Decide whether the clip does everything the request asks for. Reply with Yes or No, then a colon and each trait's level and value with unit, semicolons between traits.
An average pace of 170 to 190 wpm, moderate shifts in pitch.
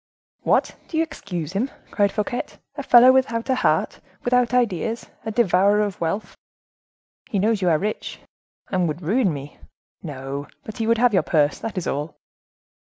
No: average, 175 wpm; wide, 5.7 semitones